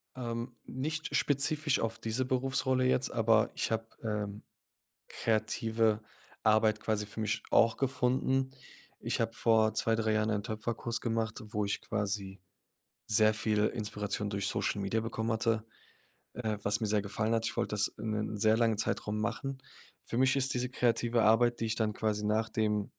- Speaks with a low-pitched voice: Yes, low, 110 Hz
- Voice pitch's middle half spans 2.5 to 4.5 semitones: No, narrow, 1.9 semitones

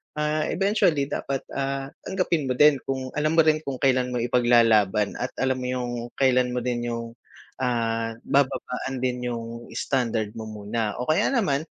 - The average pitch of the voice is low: Yes, low, 125 Hz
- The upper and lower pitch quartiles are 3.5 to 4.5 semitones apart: No, average, 2.9 semitones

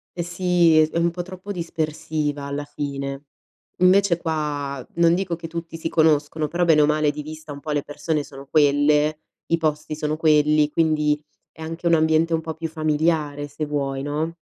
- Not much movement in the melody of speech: Yes, narrow, 1.9 semitones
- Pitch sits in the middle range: Yes, medium, 155 Hz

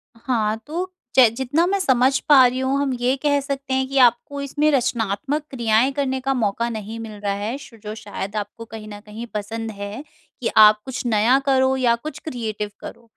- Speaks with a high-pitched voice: Yes, high, 245 Hz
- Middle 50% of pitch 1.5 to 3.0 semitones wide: No, average, 3.7 semitones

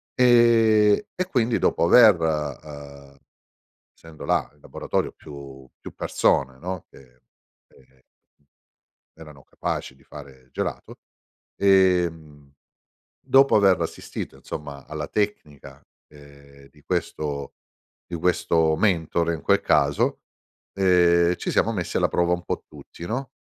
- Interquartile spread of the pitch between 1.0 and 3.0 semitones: No, average, 5.1 semitones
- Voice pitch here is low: Yes, very low, 80 Hz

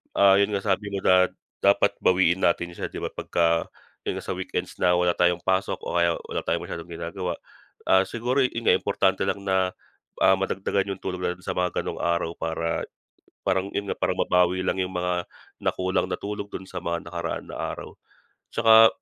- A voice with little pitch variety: Yes, narrow, 1.9 semitones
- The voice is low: Yes, very low, 95 Hz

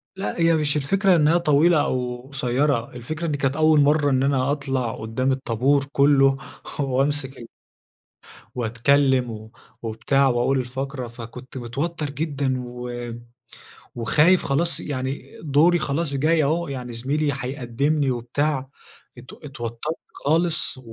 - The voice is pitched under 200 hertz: Yes, low, 135 Hz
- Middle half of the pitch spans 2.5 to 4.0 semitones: Yes, average, 3.3 semitones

